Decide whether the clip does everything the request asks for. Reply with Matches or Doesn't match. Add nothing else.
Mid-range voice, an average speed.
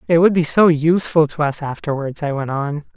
Doesn't match